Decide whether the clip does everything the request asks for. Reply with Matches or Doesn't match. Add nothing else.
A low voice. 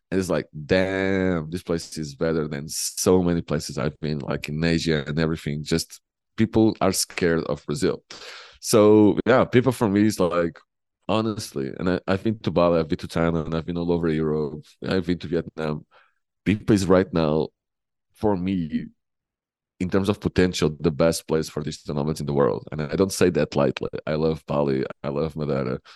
Matches